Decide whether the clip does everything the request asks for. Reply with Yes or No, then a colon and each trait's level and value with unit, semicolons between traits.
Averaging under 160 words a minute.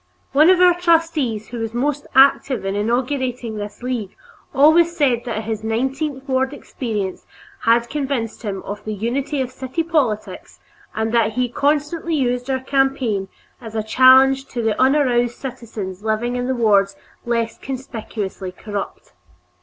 Yes: average, 145 wpm